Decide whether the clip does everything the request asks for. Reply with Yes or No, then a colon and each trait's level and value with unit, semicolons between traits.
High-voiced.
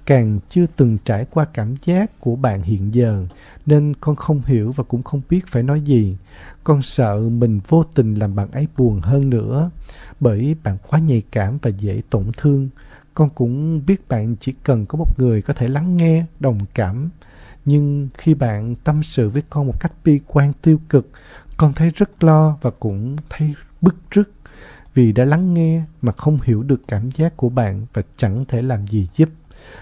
No: low, 135 Hz